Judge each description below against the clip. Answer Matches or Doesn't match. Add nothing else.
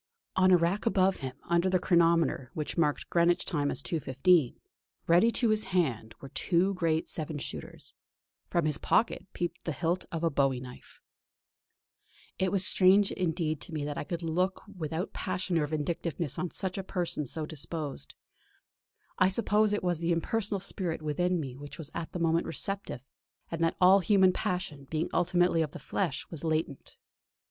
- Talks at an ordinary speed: Matches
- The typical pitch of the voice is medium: Matches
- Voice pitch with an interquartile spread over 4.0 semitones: Doesn't match